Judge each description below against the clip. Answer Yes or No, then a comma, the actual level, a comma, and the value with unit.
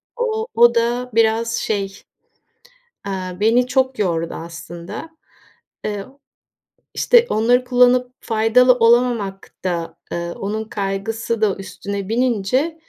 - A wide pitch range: No, average, 4.1 semitones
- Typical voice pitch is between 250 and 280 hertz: No, high, 225 Hz